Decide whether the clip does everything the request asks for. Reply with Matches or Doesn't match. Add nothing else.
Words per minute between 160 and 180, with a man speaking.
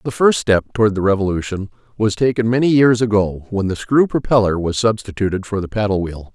Doesn't match